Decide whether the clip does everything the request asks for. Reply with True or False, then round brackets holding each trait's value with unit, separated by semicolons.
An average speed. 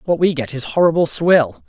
False (215 wpm)